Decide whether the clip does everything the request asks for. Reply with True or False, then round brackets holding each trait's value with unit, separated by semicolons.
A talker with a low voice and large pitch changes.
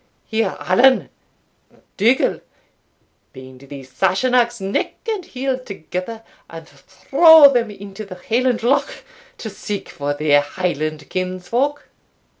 False (200 Hz; 7.7 semitones)